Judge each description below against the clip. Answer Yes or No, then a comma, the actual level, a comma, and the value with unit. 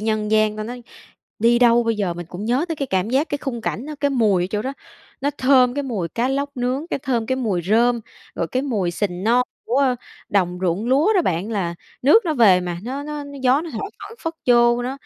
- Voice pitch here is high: Yes, high, 240 Hz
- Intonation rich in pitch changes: No, average, 4.7 semitones